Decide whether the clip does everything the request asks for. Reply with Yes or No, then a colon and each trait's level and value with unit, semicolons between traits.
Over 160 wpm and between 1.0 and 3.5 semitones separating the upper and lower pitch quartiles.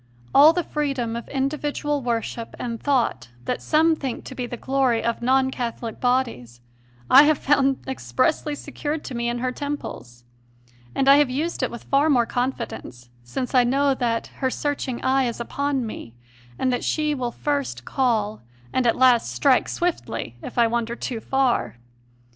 Yes: average, 170 wpm; average, 3.1 semitones